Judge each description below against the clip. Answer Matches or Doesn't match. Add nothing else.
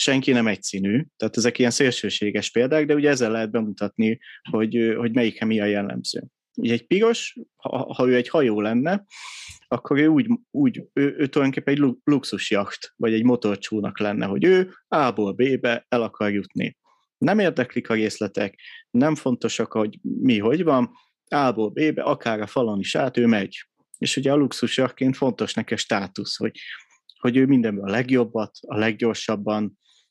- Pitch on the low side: Matches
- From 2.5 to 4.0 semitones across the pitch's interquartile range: Doesn't match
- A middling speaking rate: Doesn't match